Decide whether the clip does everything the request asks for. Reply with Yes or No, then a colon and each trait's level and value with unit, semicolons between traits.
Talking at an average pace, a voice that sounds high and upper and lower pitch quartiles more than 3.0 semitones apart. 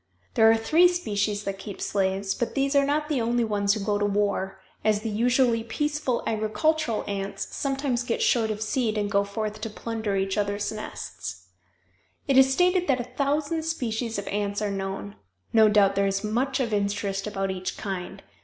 Yes: average, 190 wpm; high, 215 Hz; average, 4.1 semitones